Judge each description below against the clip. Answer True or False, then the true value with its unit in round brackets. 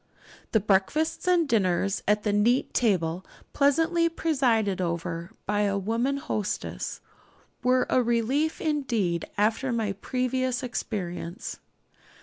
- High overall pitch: True (225 Hz)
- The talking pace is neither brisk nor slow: False (115 wpm)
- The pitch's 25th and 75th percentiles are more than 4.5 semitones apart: True (5.2 semitones)